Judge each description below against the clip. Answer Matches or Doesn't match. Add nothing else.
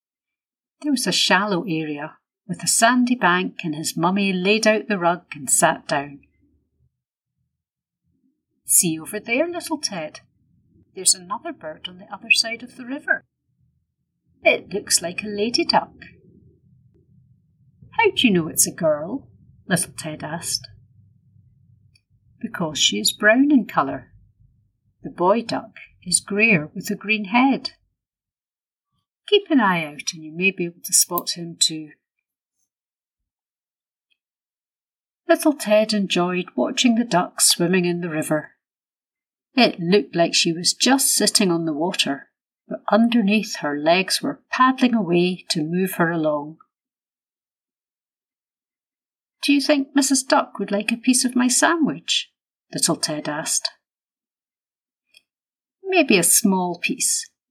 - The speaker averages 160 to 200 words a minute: Doesn't match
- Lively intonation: Matches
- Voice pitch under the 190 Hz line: Doesn't match